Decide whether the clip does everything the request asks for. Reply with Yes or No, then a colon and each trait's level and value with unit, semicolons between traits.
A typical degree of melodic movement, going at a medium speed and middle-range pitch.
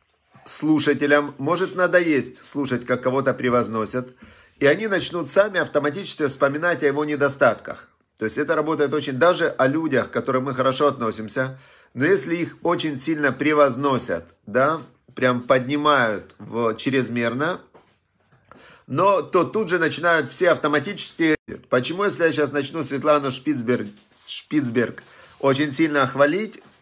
Yes: average, 3.5 semitones; average, 130 wpm; medium, 145 Hz